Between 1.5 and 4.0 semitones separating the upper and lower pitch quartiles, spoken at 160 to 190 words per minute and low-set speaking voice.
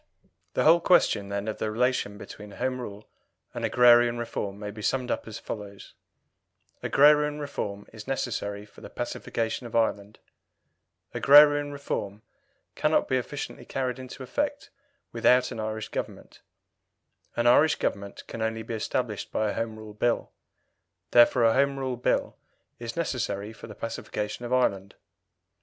No: average, 3.6 semitones; average, 150 wpm; low, 115 Hz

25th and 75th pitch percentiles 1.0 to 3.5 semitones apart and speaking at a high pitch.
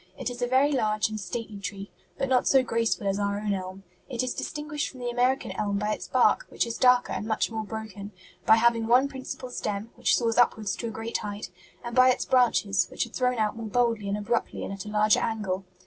Yes: average, 3.1 semitones; high, 225 Hz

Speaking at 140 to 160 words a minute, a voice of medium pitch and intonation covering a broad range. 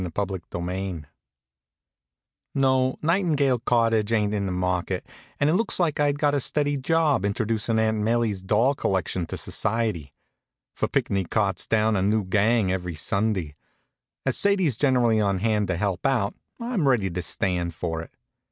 No: average, 155 wpm; low, 110 Hz; wide, 5.8 semitones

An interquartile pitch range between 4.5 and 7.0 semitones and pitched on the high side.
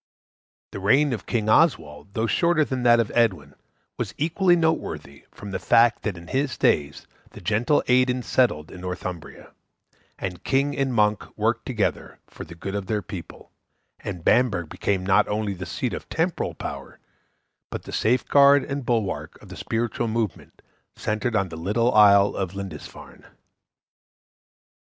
No: average, 5.1 semitones; low, 110 Hz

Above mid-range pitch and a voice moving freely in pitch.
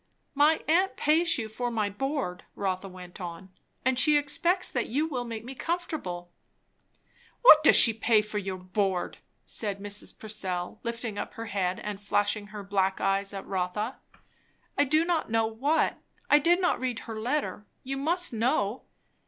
Yes: high, 225 Hz; wide, 6.6 semitones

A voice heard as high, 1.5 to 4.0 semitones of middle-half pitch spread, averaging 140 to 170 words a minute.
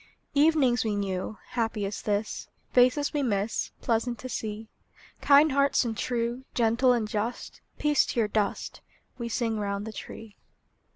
Yes: high, 230 Hz; average, 3.1 semitones; average, 155 wpm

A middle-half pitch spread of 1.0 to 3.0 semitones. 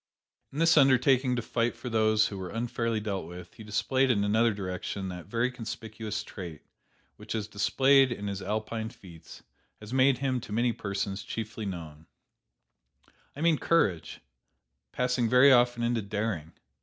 No: average, 3.8 semitones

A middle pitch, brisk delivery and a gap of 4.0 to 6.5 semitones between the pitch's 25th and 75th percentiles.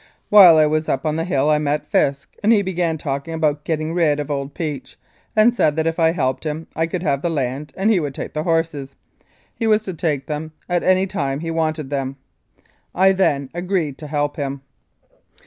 No: medium, 155 Hz; fast, 210 wpm; average, 3.2 semitones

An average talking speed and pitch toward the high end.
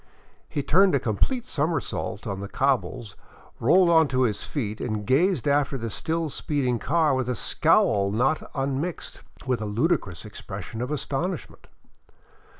No: average, 150 wpm; low, 135 Hz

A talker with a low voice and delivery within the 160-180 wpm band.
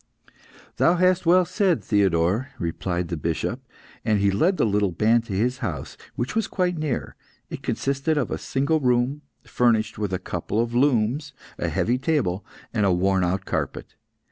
Yes: low, 115 Hz; average, 170 wpm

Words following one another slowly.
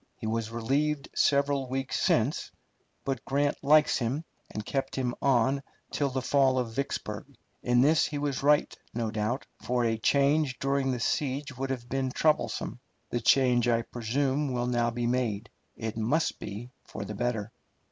No: average, 165 wpm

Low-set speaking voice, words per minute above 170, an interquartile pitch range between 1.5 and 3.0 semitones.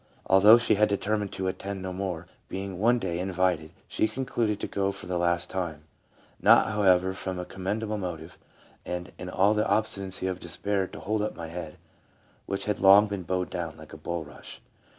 Yes: very low, 95 Hz; average, 195 wpm; narrow, 2.6 semitones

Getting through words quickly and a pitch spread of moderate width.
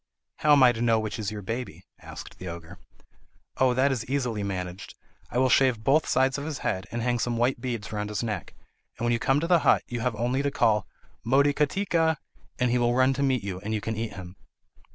Yes: fast, 235 wpm; average, 3.8 semitones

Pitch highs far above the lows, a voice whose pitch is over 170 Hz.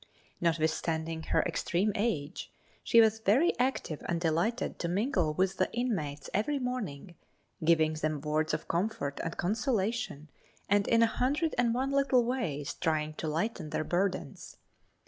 Yes: wide, 6.8 semitones; medium, 185 Hz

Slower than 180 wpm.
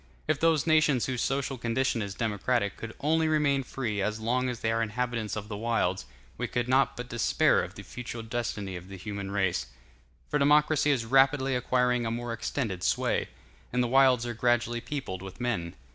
No: average, 190 wpm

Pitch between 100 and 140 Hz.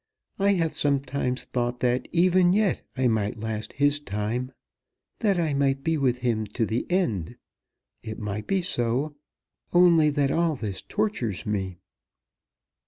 Yes: low, 135 Hz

